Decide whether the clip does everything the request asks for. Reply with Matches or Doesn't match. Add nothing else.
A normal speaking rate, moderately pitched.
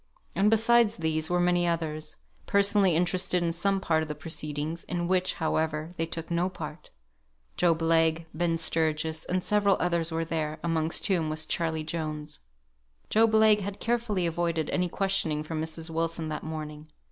Matches